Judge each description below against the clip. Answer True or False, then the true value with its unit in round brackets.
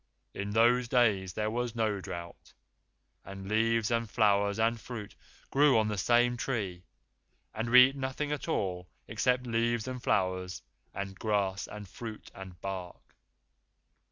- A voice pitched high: False (110 Hz)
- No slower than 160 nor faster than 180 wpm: False (145 wpm)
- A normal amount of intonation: True (3.7 semitones)